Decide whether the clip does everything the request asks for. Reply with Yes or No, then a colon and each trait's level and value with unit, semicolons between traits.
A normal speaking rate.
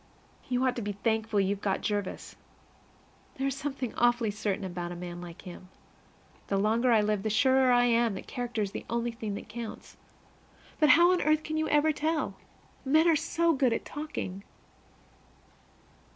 Yes: average, 180 wpm